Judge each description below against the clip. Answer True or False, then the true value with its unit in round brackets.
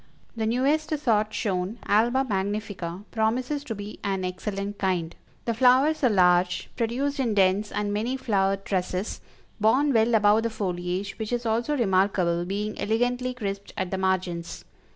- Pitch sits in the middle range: False (210 Hz)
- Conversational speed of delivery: True (150 wpm)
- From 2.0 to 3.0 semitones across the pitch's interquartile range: False (3.9 semitones)